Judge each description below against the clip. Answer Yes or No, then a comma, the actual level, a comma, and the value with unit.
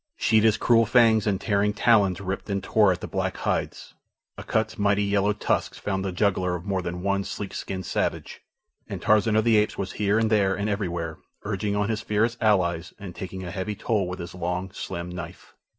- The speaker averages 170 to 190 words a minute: No, average, 200 wpm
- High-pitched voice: No, low, 100 Hz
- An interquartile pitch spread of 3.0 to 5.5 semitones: No, narrow, 2.4 semitones